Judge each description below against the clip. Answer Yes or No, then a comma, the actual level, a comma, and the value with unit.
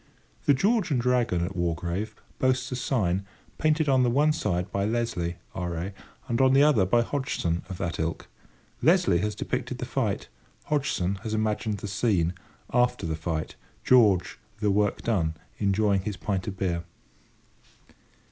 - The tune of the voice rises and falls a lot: Yes, wide, 6.0 semitones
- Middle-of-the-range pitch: No, low, 105 Hz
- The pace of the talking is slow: No, average, 155 wpm